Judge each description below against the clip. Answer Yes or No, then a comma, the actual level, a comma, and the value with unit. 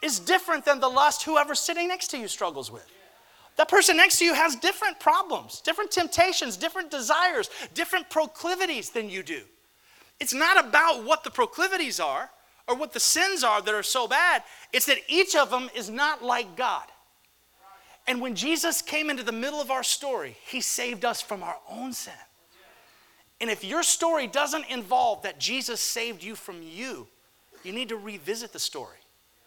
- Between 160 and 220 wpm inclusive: Yes, average, 180 wpm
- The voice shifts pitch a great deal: Yes, wide, 6.4 semitones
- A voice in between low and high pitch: No, very high, 295 Hz